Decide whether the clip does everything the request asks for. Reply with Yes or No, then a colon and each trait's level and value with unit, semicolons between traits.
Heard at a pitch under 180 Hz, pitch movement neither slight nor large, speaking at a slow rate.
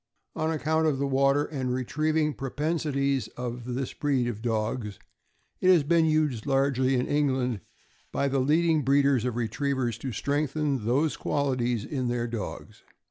No: low, 135 Hz; average, 3.2 semitones; average, 155 wpm